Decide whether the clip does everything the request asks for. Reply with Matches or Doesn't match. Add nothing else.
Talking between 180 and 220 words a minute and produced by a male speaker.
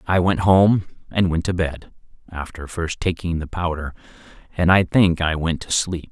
Matches